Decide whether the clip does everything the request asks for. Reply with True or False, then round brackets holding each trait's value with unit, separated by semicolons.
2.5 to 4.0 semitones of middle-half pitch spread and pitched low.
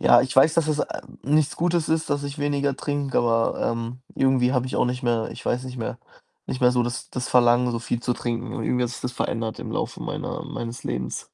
True (2.8 semitones; 125 Hz)